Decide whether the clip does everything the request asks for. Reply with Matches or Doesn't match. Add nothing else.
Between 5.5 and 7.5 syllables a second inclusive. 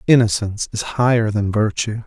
Doesn't match